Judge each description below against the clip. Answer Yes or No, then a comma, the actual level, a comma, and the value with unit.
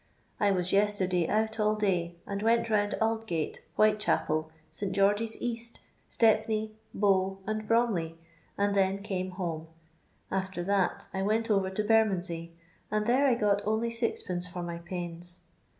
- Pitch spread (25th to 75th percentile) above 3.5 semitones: No, average, 3.2 semitones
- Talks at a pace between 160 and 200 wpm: No, average, 145 wpm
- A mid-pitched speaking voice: No, high, 200 Hz